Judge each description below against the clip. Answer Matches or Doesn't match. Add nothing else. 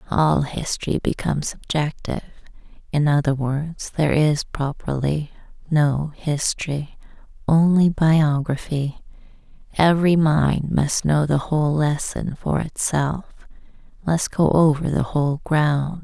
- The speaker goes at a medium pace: Doesn't match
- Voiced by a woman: Matches